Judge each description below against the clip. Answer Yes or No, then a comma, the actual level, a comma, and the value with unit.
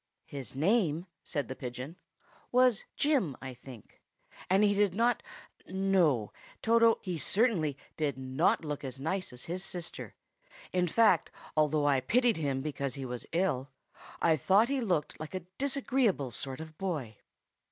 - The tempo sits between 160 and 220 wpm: No, average, 150 wpm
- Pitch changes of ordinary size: No, wide, 6.7 semitones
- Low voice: No, medium, 160 Hz